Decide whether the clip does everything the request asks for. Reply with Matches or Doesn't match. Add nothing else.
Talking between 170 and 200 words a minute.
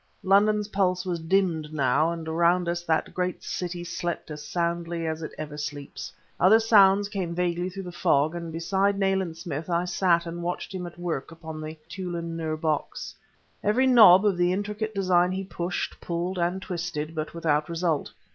Matches